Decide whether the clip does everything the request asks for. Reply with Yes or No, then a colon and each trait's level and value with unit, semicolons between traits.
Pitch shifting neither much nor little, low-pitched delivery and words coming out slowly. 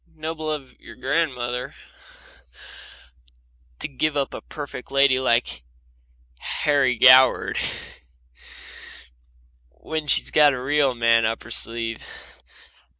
Yes: average, 3.3 semitones; low, 130 Hz; slow, 95 wpm